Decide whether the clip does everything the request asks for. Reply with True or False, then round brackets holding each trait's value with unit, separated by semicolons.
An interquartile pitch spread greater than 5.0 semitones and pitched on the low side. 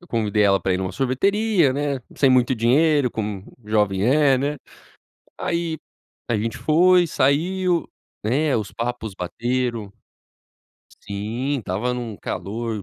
True (5.6 semitones; 125 Hz)